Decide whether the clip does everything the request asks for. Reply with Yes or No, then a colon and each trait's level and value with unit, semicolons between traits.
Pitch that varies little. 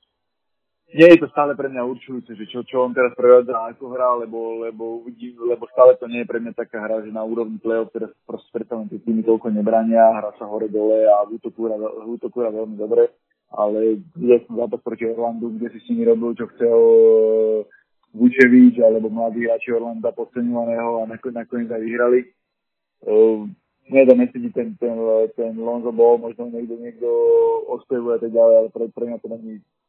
Yes: narrow, 1.9 semitones